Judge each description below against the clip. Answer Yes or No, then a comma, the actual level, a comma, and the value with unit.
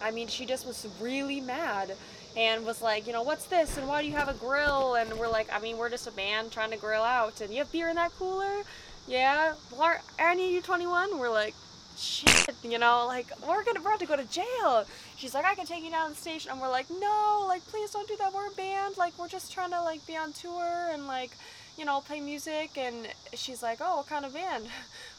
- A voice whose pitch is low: No, very high, 290 Hz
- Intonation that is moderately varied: No, wide, 6.7 semitones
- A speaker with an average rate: No, fast, 250 wpm